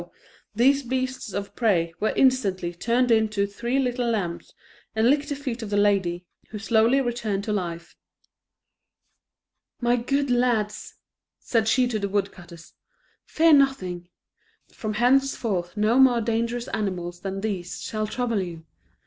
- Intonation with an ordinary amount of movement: Yes, average, 4.0 semitones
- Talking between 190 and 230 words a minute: No, average, 140 wpm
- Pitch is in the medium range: No, high, 220 Hz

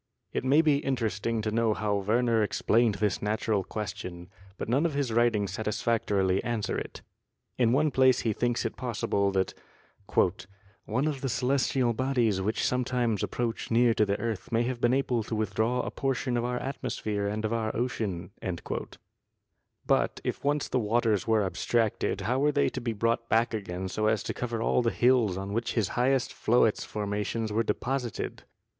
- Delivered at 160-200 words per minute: Yes, average, 180 wpm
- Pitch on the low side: Yes, low, 115 Hz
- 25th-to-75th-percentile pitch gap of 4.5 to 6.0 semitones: No, average, 2.8 semitones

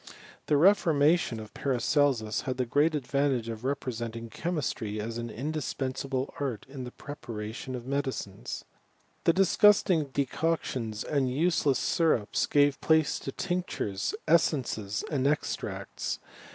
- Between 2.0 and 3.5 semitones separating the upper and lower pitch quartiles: No, average, 4.6 semitones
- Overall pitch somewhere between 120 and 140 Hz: Yes, low, 135 Hz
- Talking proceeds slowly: Yes, slow, 125 wpm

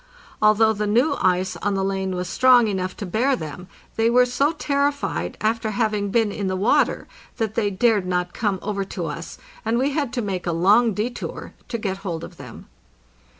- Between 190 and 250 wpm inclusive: Yes, average, 195 wpm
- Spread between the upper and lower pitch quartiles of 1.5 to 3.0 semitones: No, average, 4.0 semitones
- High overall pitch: Yes, high, 210 Hz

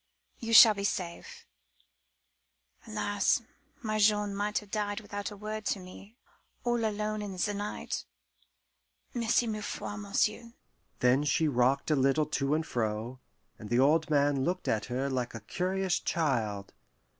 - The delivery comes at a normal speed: Yes, average, 150 wpm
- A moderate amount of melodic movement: No, wide, 7.5 semitones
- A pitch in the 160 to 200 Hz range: Yes, high, 190 Hz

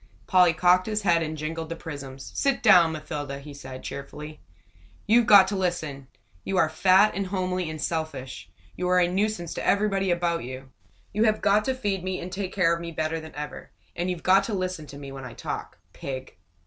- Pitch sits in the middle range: Yes, medium, 170 Hz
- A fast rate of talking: Yes, fast, 210 wpm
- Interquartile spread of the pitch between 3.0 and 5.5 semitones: Yes, average, 4.0 semitones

